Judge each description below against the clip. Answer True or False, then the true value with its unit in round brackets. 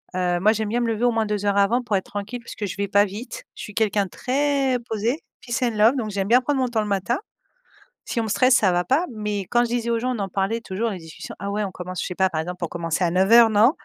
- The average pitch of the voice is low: False (210 Hz)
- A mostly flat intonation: False (3.6 semitones)